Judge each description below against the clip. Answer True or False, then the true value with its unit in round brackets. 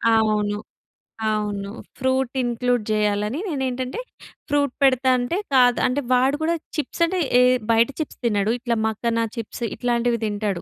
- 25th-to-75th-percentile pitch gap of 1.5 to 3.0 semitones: False (3.4 semitones)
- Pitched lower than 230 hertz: False (240 Hz)